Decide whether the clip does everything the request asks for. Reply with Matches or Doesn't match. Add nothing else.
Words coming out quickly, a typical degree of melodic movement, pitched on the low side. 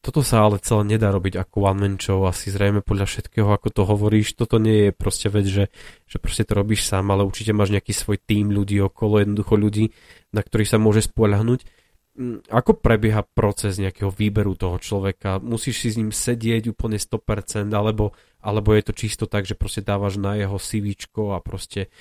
Doesn't match